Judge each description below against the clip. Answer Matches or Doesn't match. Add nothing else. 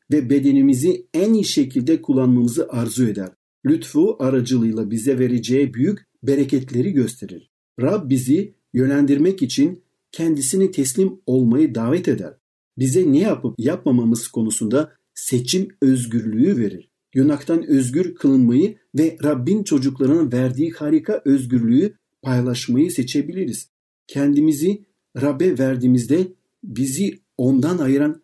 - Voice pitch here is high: Doesn't match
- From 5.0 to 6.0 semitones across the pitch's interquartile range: Matches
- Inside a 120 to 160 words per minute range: Doesn't match